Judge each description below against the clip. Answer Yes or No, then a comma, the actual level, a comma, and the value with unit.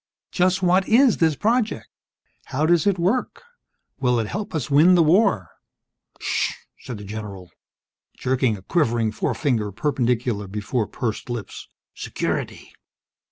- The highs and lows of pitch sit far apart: Yes, wide, 8.5 semitones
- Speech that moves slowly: Yes, slow, 130 wpm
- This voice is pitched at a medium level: No, low, 130 Hz